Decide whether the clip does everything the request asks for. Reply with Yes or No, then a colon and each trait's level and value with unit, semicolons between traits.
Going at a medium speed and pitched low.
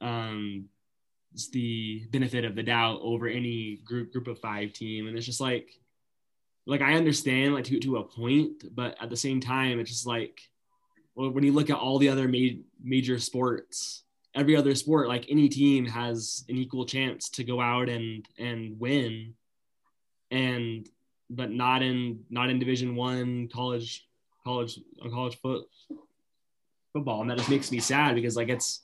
Yes: average, 175 wpm; low, 125 Hz